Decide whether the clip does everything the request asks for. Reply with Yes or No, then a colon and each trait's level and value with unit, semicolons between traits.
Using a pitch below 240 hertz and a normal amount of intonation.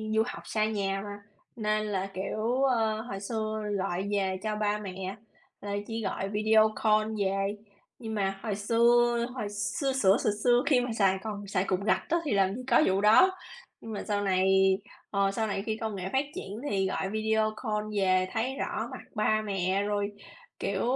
No: high, 210 Hz; narrow, 2.1 semitones